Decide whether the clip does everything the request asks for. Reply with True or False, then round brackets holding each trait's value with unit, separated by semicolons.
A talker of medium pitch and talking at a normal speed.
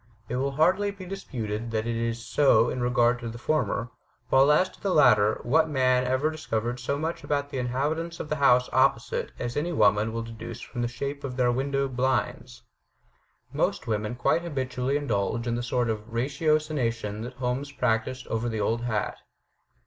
False (125 Hz; 185 wpm)